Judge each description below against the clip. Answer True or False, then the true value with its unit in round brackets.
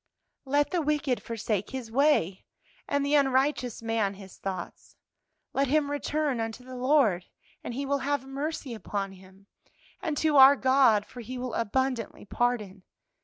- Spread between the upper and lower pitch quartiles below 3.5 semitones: False (4.5 semitones)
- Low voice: False (255 Hz)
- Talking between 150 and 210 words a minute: True (155 wpm)